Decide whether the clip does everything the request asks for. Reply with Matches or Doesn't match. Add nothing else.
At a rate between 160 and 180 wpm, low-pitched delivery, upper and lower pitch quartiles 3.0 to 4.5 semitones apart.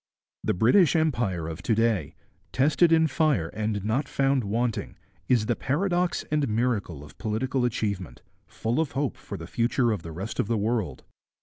Doesn't match